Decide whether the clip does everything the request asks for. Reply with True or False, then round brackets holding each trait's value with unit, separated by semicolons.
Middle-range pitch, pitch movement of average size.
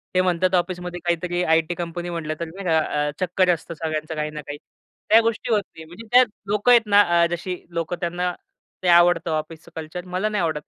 False (175 Hz; 2.2 semitones)